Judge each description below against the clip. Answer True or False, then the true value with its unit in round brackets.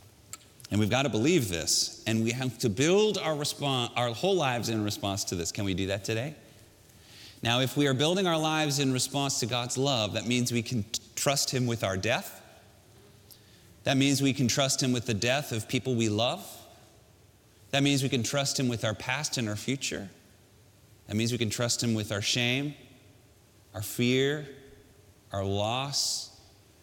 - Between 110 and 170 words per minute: False (190 wpm)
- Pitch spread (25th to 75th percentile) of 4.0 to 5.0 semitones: True (4.3 semitones)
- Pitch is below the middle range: True (120 Hz)